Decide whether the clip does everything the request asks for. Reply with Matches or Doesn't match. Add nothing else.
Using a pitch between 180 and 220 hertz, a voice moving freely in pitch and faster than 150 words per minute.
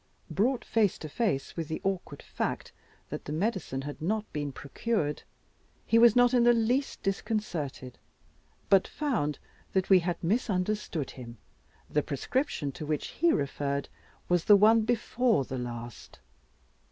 Doesn't match